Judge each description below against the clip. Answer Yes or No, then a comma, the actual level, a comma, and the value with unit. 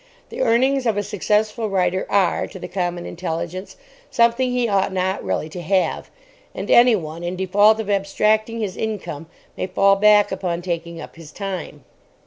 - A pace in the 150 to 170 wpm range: Yes, average, 165 wpm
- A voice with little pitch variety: No, average, 3.5 semitones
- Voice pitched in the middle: No, high, 195 Hz